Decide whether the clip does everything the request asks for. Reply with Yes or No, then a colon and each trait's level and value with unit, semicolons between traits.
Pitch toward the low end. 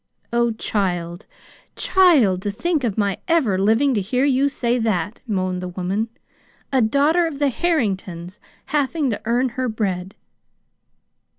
No: high, 225 Hz